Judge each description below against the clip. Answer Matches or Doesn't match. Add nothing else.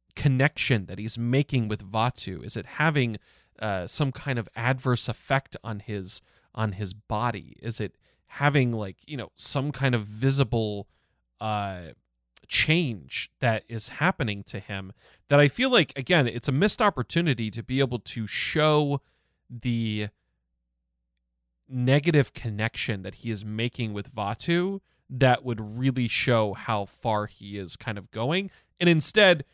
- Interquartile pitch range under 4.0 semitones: Doesn't match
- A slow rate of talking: Doesn't match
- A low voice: Matches